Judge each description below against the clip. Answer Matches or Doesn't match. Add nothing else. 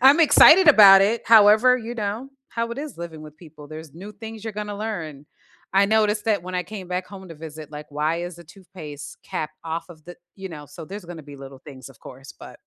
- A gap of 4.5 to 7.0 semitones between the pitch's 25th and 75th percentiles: Matches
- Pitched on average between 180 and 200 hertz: Matches